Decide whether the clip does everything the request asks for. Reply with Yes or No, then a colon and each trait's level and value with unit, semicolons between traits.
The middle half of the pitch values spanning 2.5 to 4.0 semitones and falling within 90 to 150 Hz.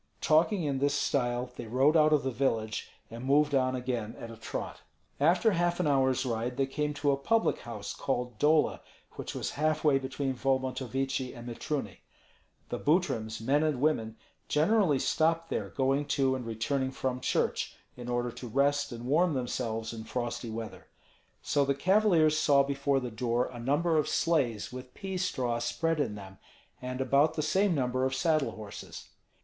Yes: average, 3.7 semitones; low, 135 Hz